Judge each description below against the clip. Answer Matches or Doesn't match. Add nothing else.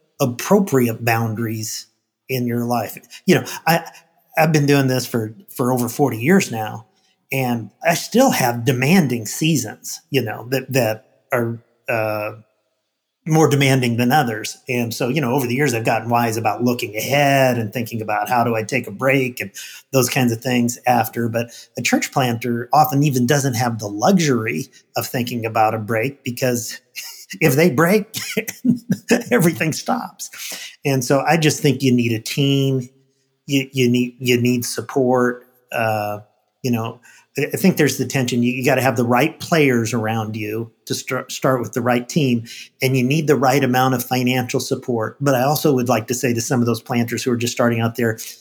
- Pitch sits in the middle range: Doesn't match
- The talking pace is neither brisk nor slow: Matches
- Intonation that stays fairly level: Doesn't match